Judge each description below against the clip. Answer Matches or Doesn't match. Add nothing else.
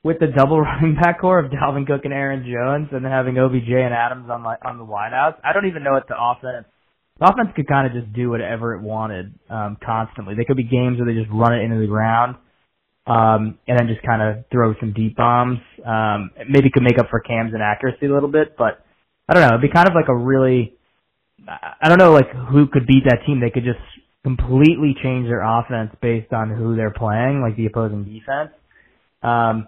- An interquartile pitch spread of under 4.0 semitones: Matches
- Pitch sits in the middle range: Doesn't match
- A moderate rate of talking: Doesn't match